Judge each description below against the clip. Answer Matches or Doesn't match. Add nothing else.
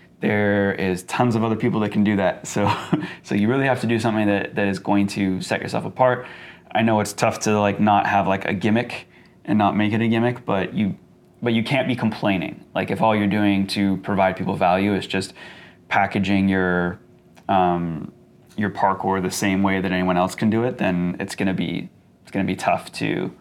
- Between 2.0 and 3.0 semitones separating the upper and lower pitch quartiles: Matches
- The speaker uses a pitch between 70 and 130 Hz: Matches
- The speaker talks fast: Matches